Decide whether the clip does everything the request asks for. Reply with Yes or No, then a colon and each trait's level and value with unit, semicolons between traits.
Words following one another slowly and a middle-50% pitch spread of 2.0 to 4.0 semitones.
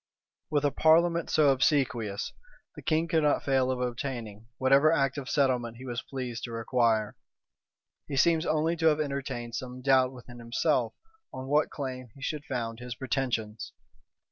No: average, 165 wpm; average, 3.5 semitones